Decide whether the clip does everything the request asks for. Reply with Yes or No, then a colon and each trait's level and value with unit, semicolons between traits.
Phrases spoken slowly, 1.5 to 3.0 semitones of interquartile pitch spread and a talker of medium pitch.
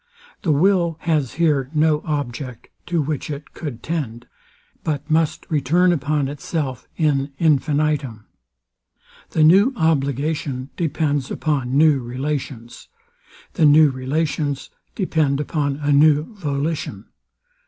Yes: slow, 110 wpm; narrow, 2.6 semitones; medium, 150 Hz